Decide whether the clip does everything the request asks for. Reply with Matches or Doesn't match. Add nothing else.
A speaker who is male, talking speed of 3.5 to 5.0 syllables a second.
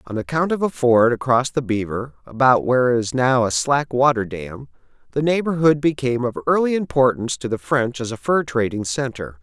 Doesn't match